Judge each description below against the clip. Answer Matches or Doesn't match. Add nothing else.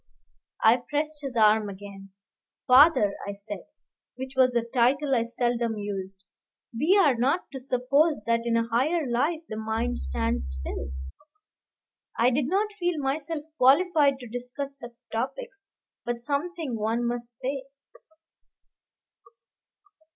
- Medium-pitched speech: Doesn't match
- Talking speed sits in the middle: Doesn't match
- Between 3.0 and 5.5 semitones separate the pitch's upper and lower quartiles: Matches